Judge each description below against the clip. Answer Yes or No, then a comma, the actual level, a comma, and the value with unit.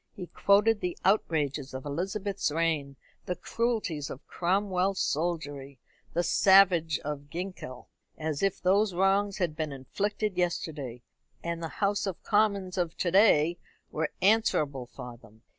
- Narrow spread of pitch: No, average, 5.0 semitones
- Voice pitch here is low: No, medium, 175 Hz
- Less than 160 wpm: Yes, average, 140 wpm